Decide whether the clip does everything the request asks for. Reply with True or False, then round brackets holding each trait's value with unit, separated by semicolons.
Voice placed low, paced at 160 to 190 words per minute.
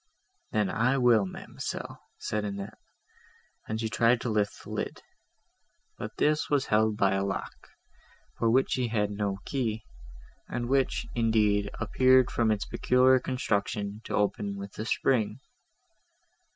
False (110 Hz; 140 wpm)